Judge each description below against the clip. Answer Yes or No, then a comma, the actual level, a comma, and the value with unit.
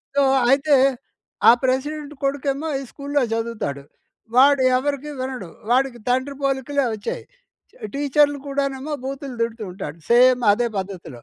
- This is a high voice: Yes, very high, 265 Hz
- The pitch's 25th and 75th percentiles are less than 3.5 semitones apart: Yes, average, 2.9 semitones